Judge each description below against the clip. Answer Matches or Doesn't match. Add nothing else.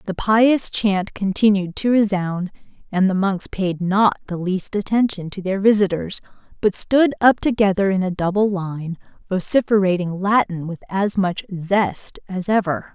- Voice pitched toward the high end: Matches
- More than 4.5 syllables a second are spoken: Doesn't match